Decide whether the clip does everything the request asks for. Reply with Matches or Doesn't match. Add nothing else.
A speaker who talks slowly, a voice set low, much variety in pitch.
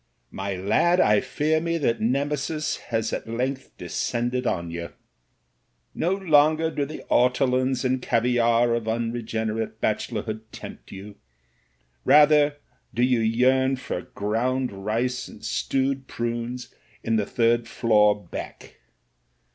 Doesn't match